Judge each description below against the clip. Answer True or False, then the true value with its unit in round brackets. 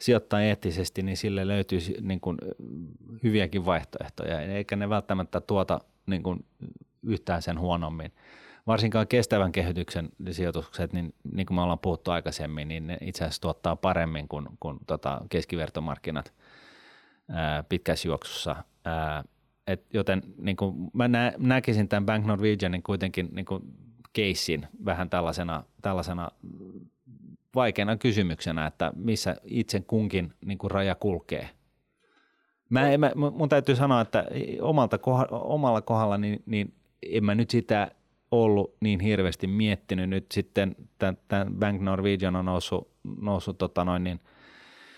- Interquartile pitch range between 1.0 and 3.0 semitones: False (3.5 semitones)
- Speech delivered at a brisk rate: False (135 wpm)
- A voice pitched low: True (95 Hz)